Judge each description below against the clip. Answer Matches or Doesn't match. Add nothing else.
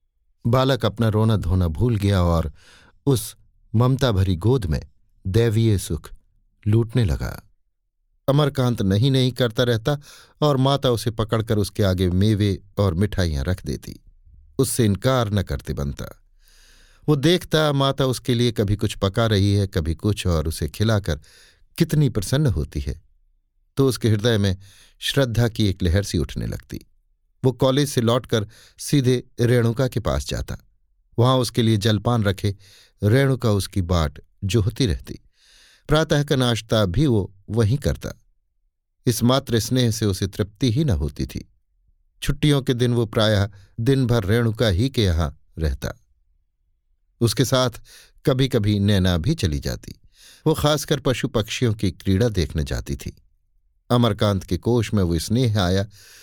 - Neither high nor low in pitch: Doesn't match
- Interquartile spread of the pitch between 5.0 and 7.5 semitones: Matches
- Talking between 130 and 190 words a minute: Matches